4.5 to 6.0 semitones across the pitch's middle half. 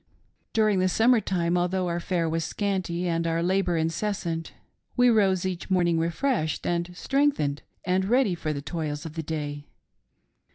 No: average, 2.8 semitones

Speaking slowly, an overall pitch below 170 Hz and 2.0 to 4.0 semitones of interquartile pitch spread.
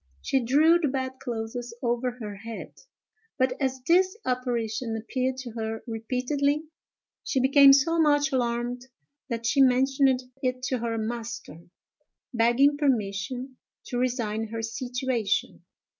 No: slow, 130 wpm; very high, 250 Hz; narrow, 2.6 semitones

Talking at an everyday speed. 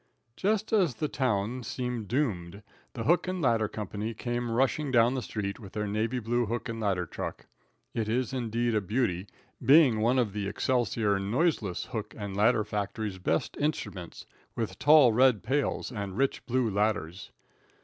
Yes: average, 165 wpm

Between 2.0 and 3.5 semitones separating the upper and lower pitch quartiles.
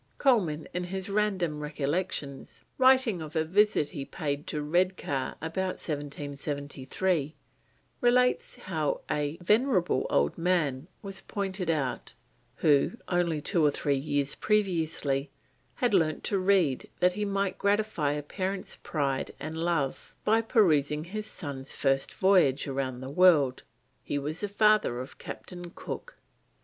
No: wide, 5.4 semitones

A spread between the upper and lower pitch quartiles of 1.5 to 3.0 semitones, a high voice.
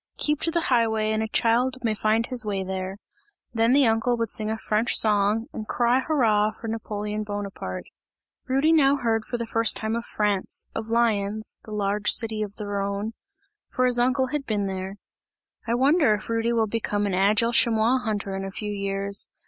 Yes: narrow, 2.5 semitones; high, 220 Hz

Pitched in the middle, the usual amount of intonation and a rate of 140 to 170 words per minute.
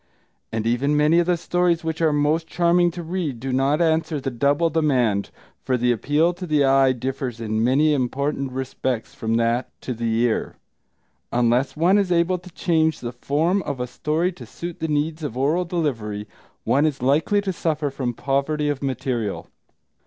No: medium, 145 Hz; average, 4.7 semitones; average, 180 wpm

